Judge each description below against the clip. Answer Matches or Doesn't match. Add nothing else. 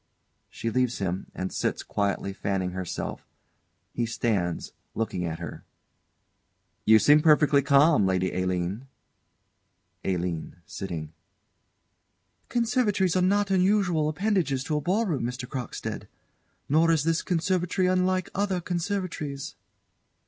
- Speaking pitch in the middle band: Matches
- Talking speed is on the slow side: Matches